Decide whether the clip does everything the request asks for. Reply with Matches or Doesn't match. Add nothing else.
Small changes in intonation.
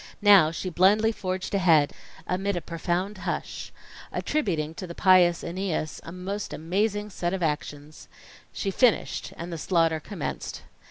Doesn't match